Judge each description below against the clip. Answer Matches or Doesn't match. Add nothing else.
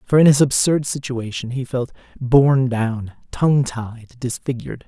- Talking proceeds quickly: Doesn't match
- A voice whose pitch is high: Doesn't match